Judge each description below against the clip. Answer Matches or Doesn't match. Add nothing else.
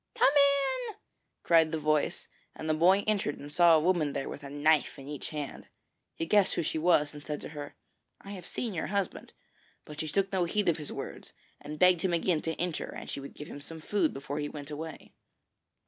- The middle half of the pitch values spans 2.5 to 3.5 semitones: Doesn't match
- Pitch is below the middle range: Doesn't match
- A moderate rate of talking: Doesn't match